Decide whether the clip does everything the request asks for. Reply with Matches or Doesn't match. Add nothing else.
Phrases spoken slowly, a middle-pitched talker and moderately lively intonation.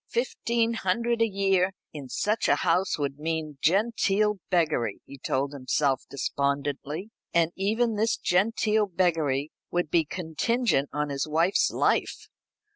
Doesn't match